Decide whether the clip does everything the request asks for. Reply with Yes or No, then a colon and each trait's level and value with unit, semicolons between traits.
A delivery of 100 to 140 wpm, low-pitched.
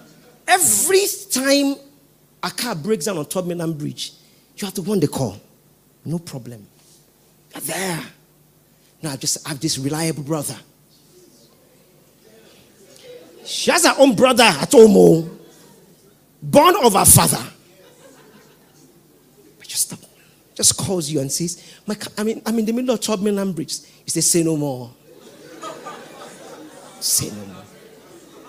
No: slow, 135 wpm; medium, 175 Hz